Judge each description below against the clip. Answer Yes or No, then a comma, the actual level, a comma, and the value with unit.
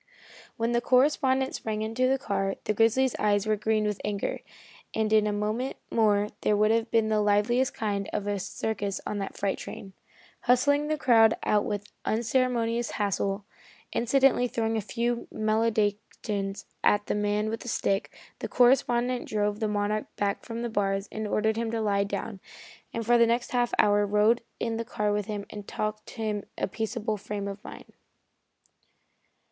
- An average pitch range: No, narrow, 2.2 semitones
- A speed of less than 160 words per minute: No, average, 175 wpm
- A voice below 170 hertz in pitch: No, high, 215 Hz